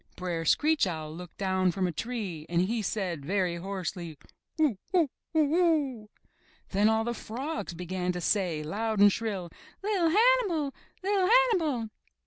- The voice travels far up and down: Yes, wide, 8.7 semitones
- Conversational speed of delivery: Yes, average, 150 wpm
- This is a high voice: Yes, high, 210 Hz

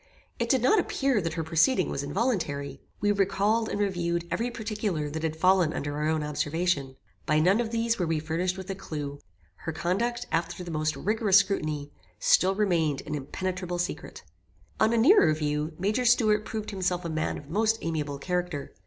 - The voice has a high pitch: No, medium, 180 Hz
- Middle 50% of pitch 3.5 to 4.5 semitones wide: No, average, 5.3 semitones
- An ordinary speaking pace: Yes, average, 185 wpm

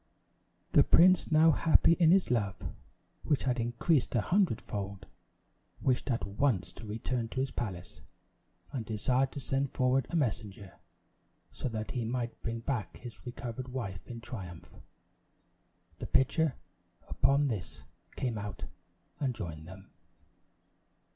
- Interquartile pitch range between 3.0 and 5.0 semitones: Yes, average, 4.4 semitones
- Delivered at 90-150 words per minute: Yes, slow, 135 wpm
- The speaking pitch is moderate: No, low, 120 Hz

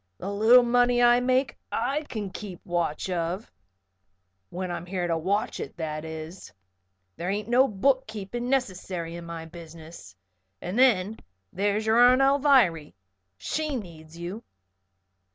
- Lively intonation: Yes, wide, 6.2 semitones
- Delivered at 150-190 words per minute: No, average, 140 wpm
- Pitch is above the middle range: Yes, high, 195 Hz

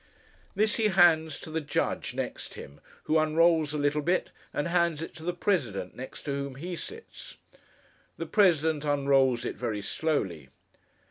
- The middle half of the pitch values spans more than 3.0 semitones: Yes, average, 3.6 semitones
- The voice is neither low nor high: Yes, medium, 155 Hz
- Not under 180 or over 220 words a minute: No, average, 160 wpm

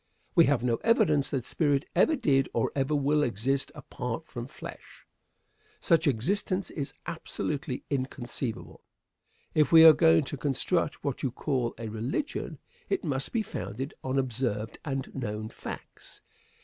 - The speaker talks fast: No, average, 145 wpm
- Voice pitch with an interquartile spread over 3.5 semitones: Yes, average, 3.9 semitones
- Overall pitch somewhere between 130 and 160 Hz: Yes, low, 135 Hz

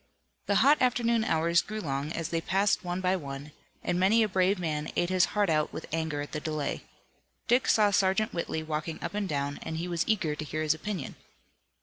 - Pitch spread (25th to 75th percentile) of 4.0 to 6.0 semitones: Yes, average, 4.7 semitones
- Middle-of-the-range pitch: Yes, medium, 175 Hz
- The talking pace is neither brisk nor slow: No, fast, 215 wpm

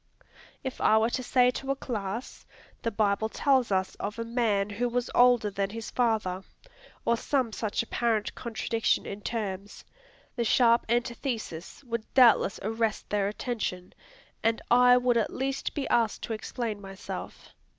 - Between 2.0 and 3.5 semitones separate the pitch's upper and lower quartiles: Yes, average, 2.9 semitones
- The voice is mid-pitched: No, high, 230 Hz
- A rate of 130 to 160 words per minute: Yes, average, 155 wpm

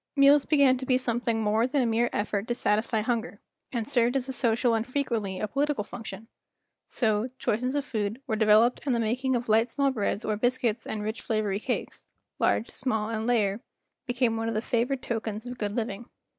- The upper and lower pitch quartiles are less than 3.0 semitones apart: Yes, narrow, 2.6 semitones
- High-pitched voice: Yes, high, 230 Hz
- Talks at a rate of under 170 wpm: No, average, 200 wpm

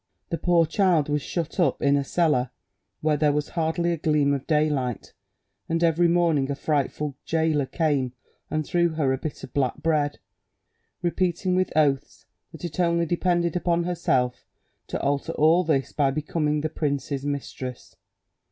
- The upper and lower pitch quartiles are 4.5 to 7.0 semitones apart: No, average, 3.1 semitones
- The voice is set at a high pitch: No, medium, 155 Hz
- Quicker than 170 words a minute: No, average, 160 wpm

